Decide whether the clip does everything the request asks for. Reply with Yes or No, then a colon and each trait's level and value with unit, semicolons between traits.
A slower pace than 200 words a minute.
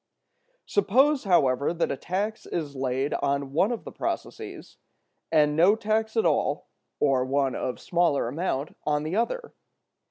Yes: average, 150 wpm